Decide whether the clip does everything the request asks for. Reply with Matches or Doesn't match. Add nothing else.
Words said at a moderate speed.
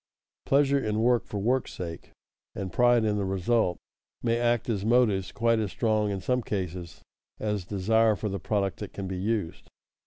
Matches